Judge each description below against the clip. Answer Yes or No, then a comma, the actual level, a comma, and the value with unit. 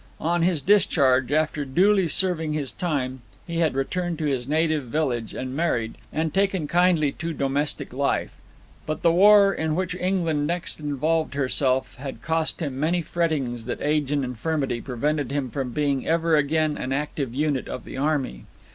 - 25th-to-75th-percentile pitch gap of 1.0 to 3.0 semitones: No, average, 3.6 semitones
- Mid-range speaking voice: Yes, medium, 150 Hz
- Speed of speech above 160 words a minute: Yes, average, 170 wpm